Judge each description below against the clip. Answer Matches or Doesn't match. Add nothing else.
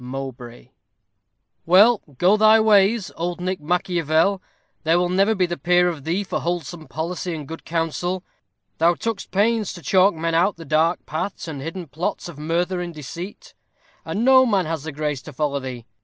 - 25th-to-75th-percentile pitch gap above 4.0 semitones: Doesn't match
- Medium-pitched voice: Matches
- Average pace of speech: Matches